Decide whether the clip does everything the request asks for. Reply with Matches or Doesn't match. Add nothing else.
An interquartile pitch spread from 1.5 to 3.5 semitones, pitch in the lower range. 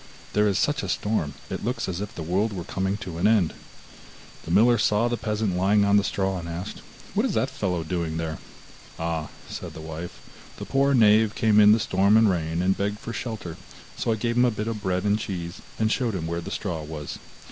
Doesn't match